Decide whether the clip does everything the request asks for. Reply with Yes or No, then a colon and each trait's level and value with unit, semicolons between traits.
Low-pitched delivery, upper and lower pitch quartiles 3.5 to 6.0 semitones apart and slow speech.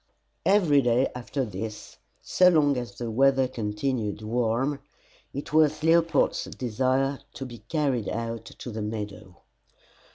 Yes: low, 125 Hz; average, 4.0 semitones; slow, 130 wpm